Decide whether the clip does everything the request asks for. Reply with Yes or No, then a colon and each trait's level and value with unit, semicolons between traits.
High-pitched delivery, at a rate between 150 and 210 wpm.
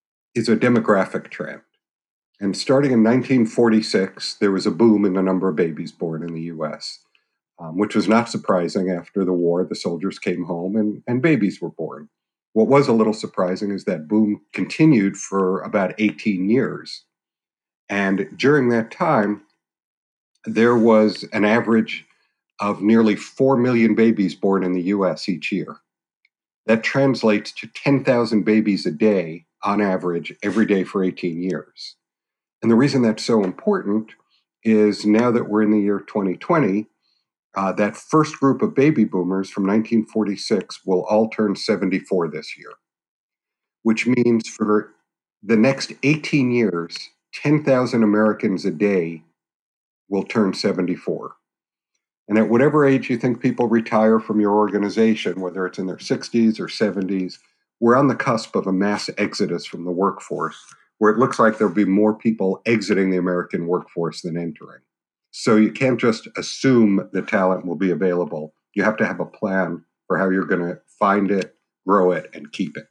No: low, 105 Hz; average, 165 wpm